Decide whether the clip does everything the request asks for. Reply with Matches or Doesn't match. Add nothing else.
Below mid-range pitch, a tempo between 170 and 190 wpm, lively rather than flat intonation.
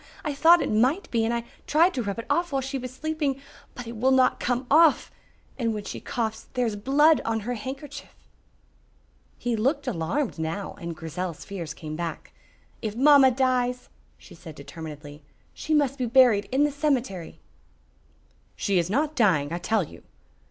Doesn't match